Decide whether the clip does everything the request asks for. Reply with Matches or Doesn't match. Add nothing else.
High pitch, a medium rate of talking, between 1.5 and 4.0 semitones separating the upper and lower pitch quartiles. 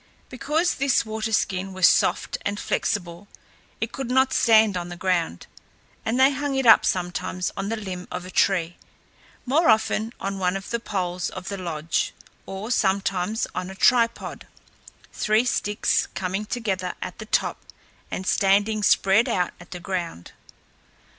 Matches